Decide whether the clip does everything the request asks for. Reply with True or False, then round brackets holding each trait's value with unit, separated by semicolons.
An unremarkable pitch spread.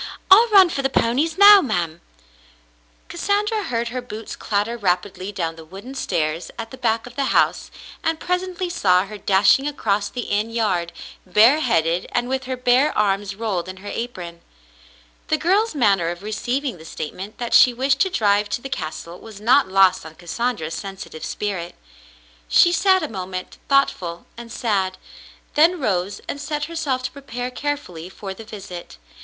False (6.7 semitones)